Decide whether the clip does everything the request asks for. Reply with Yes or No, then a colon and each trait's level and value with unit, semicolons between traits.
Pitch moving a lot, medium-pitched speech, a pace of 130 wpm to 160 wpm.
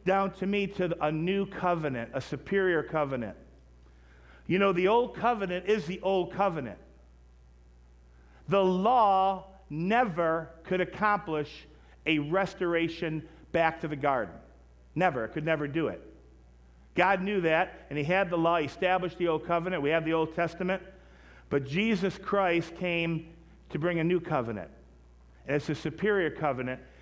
Yes: wide, 6.5 semitones; medium, 165 Hz; average, 150 wpm